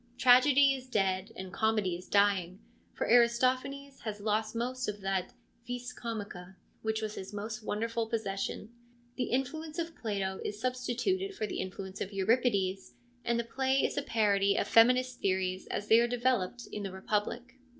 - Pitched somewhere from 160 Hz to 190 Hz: No, high, 225 Hz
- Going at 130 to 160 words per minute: No, average, 175 wpm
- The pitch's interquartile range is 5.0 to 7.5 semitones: No, average, 4.1 semitones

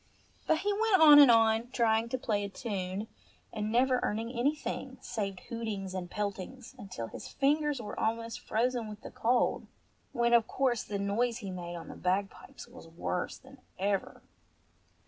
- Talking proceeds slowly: No, average, 165 wpm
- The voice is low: No, high, 225 Hz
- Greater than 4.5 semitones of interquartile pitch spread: No, average, 4.0 semitones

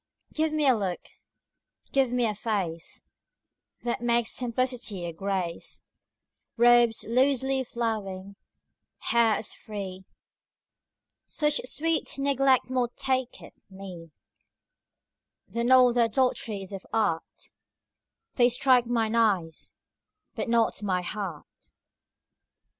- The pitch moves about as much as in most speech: Yes, average, 4.5 semitones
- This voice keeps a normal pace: No, slow, 105 wpm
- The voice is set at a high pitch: Yes, high, 235 Hz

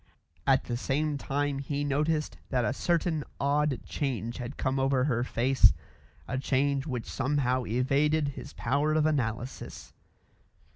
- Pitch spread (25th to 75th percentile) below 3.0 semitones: Yes, narrow, 2.4 semitones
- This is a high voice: No, low, 135 Hz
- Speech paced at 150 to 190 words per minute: No, average, 140 wpm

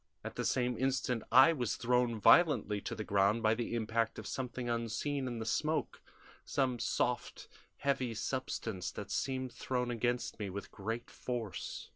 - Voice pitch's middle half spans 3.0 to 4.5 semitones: No, narrow, 2.5 semitones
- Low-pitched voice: Yes, low, 120 Hz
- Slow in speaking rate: No, average, 160 wpm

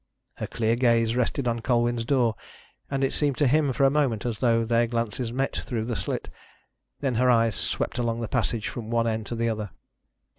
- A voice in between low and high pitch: No, low, 120 Hz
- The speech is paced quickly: Yes, fast, 210 wpm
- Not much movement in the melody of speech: Yes, narrow, 1.8 semitones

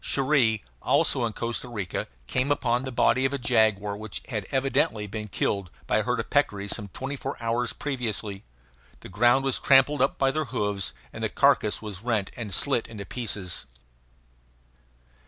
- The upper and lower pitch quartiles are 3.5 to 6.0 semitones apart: Yes, average, 4.2 semitones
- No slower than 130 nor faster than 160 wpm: No, average, 175 wpm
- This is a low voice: Yes, low, 115 Hz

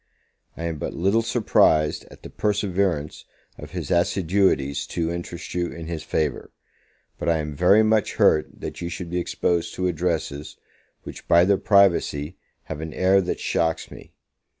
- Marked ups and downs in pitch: No, average, 3.3 semitones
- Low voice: Yes, very low, 85 Hz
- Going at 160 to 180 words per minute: Yes, average, 165 wpm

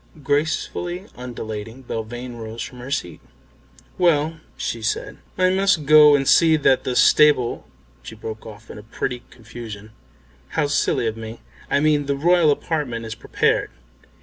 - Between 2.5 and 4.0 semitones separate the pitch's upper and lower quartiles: No, average, 5.2 semitones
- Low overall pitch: Yes, low, 125 Hz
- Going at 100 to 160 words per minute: Yes, average, 155 wpm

